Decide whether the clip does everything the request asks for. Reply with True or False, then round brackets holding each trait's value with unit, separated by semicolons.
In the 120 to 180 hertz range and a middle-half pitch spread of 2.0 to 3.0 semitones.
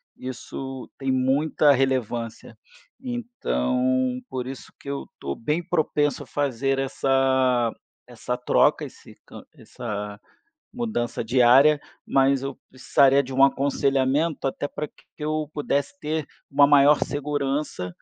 True (135 Hz; 2.4 semitones)